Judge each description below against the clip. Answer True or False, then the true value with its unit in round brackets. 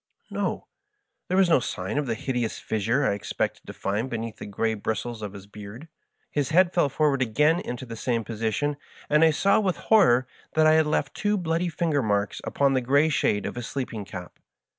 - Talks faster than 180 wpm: True (205 wpm)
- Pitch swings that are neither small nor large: False (6.1 semitones)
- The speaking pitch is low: True (130 Hz)